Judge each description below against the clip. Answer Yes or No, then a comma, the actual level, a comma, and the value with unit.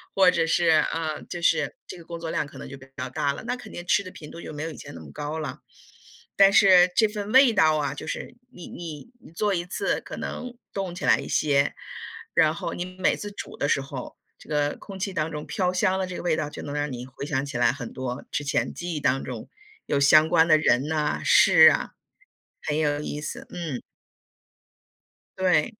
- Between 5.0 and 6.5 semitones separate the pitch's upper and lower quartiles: No, average, 3.8 semitones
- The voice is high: No, medium, 155 Hz